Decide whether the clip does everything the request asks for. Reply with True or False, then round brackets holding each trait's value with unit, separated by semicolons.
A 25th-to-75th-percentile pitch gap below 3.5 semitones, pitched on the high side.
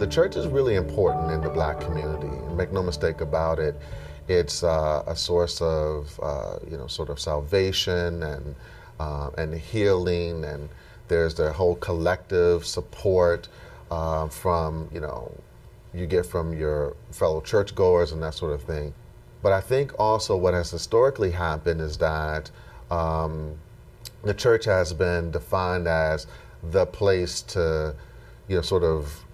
False (2.5 semitones; 80 Hz)